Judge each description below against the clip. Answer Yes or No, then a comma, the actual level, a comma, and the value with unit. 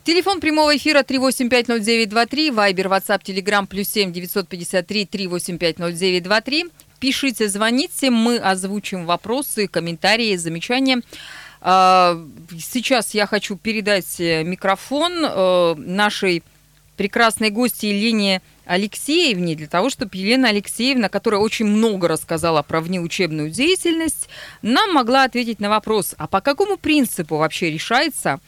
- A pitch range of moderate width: No, wide, 5.7 semitones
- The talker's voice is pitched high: Yes, high, 205 Hz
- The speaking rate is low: Yes, slow, 105 wpm